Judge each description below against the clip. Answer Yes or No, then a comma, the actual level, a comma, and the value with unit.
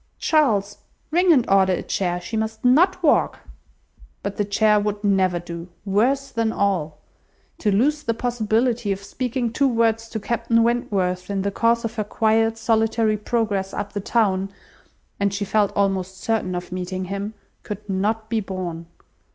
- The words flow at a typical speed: Yes, average, 165 wpm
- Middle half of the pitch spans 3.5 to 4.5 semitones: No, average, 2.9 semitones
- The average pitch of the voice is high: Yes, high, 210 Hz